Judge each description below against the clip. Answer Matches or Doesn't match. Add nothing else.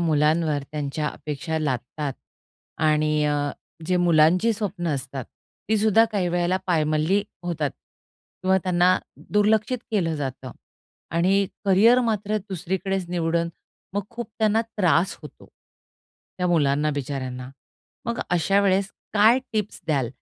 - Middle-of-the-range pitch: Matches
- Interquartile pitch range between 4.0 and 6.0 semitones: Matches